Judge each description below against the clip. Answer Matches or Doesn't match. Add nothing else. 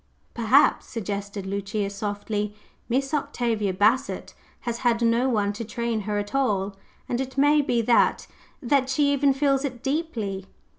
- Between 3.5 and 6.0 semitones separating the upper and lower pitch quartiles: Matches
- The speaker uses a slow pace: Doesn't match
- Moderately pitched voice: Doesn't match